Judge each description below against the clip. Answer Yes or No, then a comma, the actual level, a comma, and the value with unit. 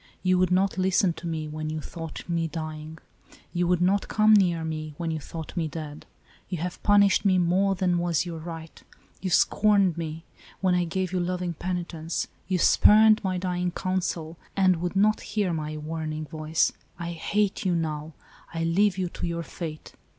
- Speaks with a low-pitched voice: No, medium, 175 Hz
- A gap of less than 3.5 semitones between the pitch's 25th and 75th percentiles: Yes, narrow, 2.5 semitones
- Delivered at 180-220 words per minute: Yes, average, 185 wpm